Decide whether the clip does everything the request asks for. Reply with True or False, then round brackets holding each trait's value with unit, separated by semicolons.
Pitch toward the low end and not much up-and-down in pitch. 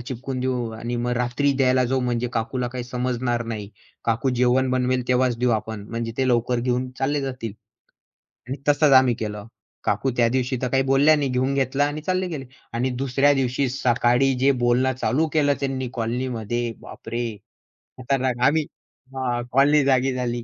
True (125 Hz; 1.8 semitones)